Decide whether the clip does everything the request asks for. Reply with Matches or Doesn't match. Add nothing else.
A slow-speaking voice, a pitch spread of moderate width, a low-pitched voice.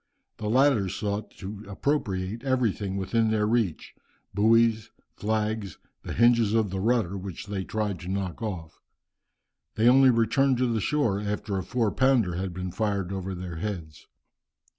Doesn't match